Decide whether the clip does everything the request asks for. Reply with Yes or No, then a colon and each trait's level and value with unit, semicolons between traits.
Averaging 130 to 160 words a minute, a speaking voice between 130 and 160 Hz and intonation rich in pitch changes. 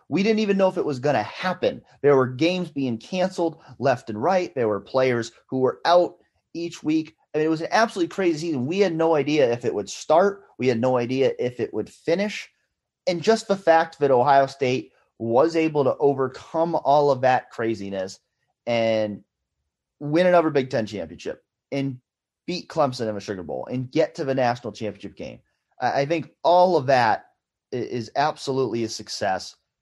No: average, 190 wpm; medium, 140 Hz; wide, 5.8 semitones